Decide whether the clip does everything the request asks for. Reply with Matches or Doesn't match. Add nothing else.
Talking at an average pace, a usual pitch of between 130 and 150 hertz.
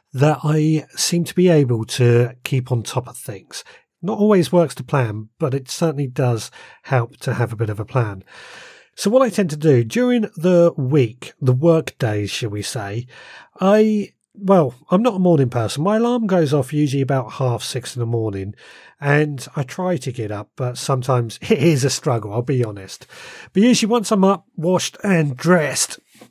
Matches